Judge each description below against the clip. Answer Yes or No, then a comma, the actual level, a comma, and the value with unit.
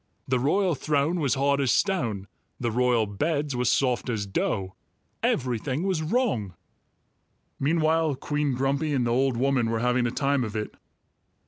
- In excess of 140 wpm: Yes, average, 155 wpm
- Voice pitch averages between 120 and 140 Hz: Yes, low, 135 Hz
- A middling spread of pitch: Yes, average, 3.9 semitones